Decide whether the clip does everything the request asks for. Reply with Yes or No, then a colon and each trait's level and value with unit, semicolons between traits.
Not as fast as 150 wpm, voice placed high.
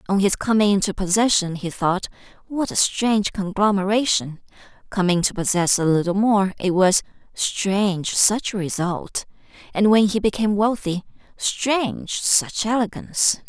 Yes: slow, 135 wpm; high, 200 Hz